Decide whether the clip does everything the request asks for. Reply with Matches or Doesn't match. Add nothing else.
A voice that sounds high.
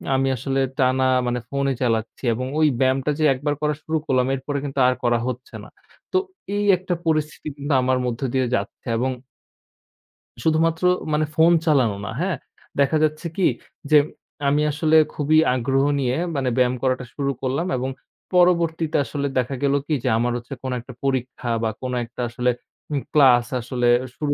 Doesn't match